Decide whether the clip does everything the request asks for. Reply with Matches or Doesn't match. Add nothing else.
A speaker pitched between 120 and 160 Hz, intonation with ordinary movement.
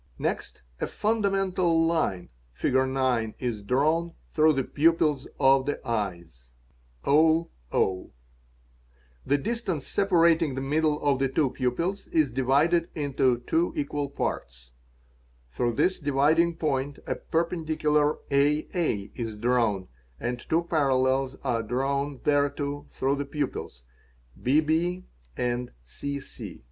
Matches